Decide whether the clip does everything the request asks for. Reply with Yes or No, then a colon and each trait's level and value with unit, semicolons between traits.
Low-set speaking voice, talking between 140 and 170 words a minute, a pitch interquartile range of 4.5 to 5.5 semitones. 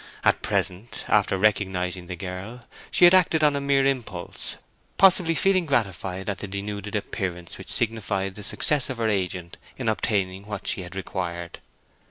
Yes: low, 100 Hz; average, 165 wpm; average, 5.1 semitones